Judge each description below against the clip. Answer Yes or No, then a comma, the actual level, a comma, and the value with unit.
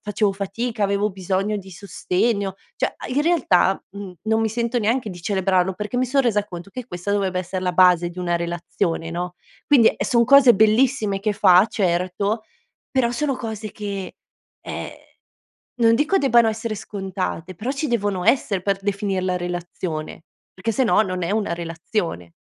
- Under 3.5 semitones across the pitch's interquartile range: No, average, 3.8 semitones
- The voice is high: Yes, high, 200 Hz